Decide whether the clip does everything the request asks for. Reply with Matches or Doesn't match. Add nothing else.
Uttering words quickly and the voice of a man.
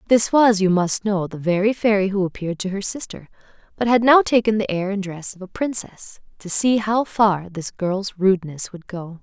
Doesn't match